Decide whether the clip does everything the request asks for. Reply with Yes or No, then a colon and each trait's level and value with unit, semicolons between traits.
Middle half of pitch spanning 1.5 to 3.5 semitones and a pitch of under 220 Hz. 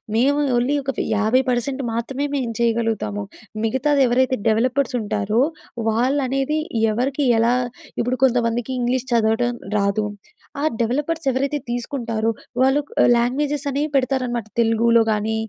No: average, 2.9 semitones; high, 245 Hz